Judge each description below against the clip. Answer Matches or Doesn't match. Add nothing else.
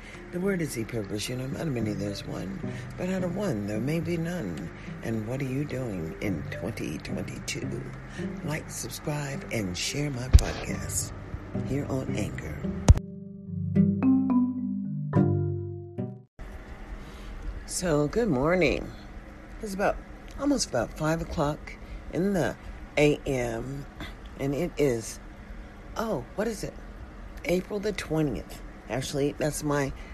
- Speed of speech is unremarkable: Doesn't match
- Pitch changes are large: Matches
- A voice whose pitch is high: Doesn't match